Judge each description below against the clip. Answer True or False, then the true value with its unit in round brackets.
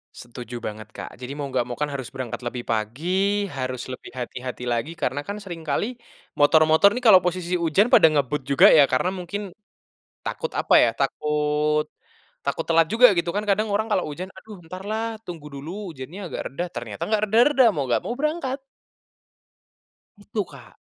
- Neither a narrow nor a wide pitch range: False (7.6 semitones)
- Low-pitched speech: False (155 Hz)